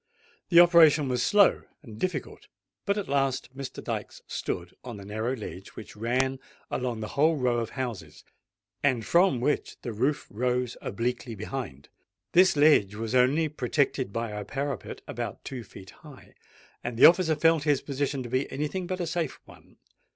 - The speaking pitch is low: Yes, low, 130 Hz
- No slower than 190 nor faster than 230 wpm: No, average, 175 wpm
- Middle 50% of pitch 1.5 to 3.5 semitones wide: No, average, 4.5 semitones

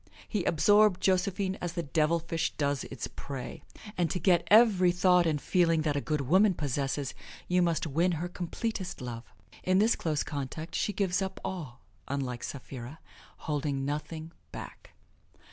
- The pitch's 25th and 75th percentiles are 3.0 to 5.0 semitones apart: Yes, average, 4.4 semitones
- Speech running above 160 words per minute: No, average, 155 wpm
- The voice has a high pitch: No, medium, 165 Hz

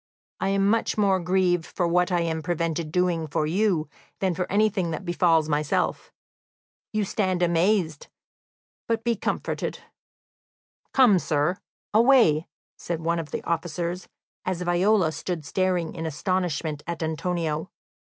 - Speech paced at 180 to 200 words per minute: No, slow, 135 wpm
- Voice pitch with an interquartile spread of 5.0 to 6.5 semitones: No, narrow, 2.6 semitones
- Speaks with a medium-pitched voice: Yes, medium, 175 Hz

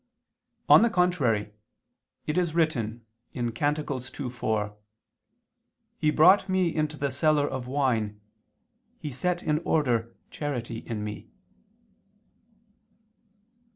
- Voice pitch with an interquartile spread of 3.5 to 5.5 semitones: Yes, average, 5.1 semitones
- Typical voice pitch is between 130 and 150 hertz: Yes, medium, 140 Hz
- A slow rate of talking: Yes, slow, 100 wpm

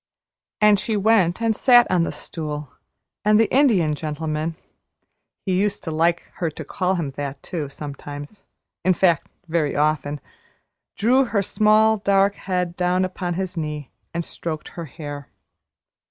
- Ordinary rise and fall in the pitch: Yes, average, 4.8 semitones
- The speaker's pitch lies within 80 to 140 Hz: No, medium, 175 Hz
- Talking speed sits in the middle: Yes, average, 150 wpm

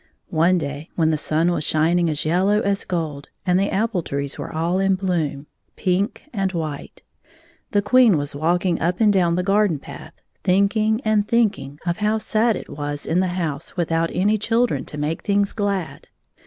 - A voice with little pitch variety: No, average, 4.3 semitones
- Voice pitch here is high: No, medium, 180 Hz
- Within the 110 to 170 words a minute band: No, average, 190 wpm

